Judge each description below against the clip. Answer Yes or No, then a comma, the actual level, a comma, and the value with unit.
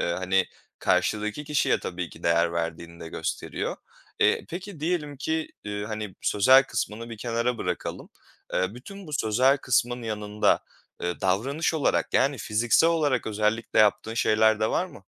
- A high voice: No, low, 110 Hz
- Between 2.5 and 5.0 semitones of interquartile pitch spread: No, wide, 5.6 semitones